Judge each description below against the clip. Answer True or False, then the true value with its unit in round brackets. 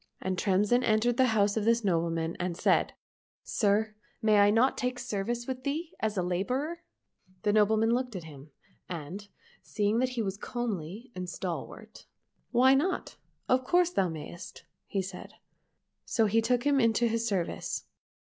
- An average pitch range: True (4.7 semitones)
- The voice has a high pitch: True (215 Hz)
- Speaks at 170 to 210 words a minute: True (175 wpm)